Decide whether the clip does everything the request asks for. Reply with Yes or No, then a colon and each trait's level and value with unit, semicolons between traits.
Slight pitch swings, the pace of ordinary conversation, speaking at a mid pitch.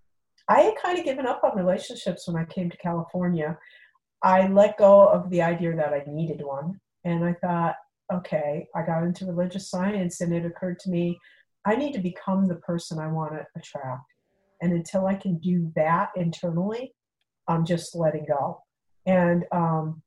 Yes: narrow, 2.3 semitones; average, 180 wpm; medium, 175 Hz